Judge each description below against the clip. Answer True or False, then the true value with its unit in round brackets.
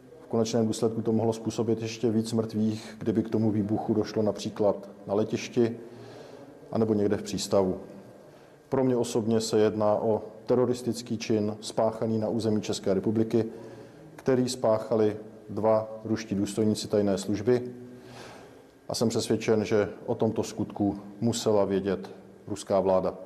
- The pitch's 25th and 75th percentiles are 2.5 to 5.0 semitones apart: False (1.5 semitones)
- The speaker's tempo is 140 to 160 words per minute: False (130 wpm)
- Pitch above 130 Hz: False (110 Hz)